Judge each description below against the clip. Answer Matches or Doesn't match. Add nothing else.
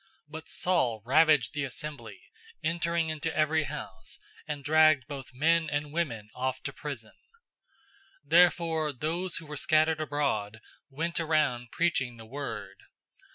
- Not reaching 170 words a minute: Matches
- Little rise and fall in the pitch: Doesn't match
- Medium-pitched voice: Matches